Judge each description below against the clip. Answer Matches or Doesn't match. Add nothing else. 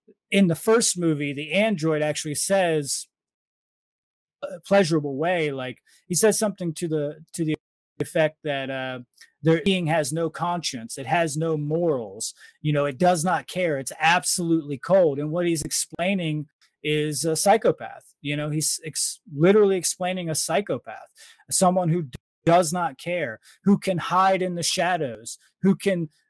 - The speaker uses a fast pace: Doesn't match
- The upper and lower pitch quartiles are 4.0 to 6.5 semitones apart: Doesn't match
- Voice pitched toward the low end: Doesn't match